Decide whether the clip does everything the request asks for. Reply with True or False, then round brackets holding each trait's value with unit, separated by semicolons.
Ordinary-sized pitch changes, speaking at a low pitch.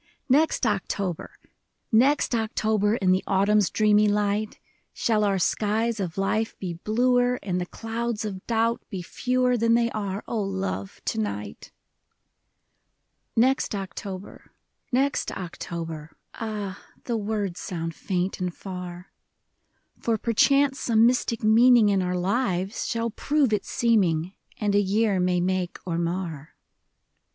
False (3.8 semitones; 205 Hz)